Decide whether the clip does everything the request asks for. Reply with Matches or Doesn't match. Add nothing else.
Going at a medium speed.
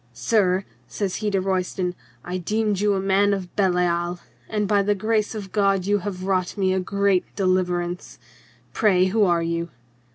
Matches